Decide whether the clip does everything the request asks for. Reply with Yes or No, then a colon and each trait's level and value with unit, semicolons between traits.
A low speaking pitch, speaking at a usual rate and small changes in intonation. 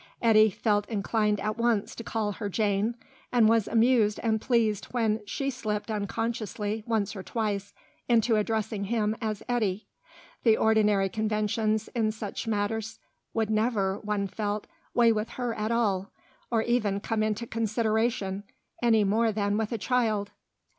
No: high, 215 Hz; average, 150 wpm; narrow, 1.7 semitones